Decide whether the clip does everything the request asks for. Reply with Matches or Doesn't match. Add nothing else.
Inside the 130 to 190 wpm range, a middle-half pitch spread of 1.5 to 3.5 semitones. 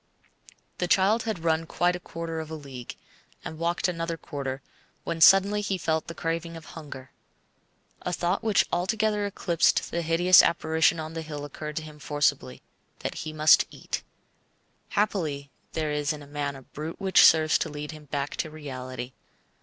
Matches